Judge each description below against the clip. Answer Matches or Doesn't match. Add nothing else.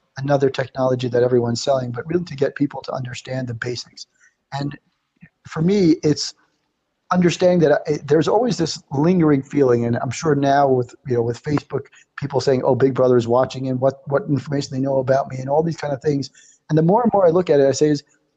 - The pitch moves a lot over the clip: Doesn't match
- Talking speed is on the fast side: Matches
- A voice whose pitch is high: Doesn't match